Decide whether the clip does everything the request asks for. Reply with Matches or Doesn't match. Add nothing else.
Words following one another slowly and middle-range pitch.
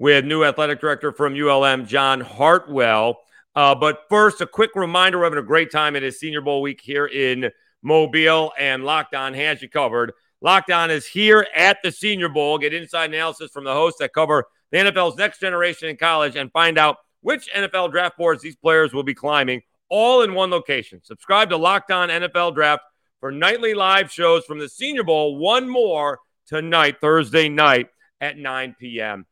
Doesn't match